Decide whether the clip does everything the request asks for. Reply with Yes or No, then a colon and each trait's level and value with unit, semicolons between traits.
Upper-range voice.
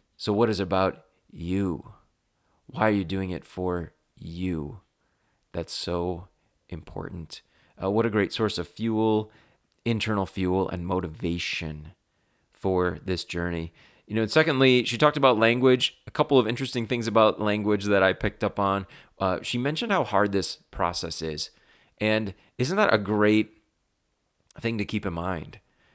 No: low, 100 Hz